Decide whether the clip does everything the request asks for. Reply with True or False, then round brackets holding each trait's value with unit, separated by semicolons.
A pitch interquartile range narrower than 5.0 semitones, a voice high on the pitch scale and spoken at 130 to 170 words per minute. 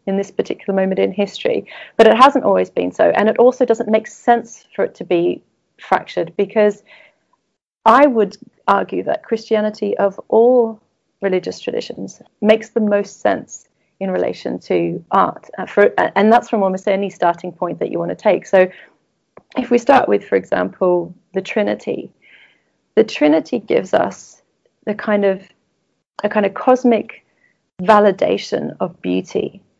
True (3.4 semitones; 210 Hz; 155 wpm)